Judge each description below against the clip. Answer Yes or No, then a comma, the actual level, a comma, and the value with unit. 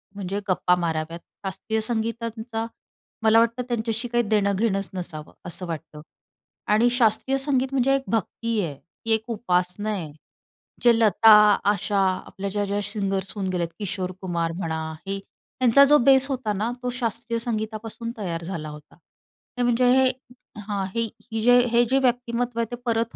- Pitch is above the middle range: Yes, high, 220 Hz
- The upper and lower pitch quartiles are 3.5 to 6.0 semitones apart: Yes, average, 3.8 semitones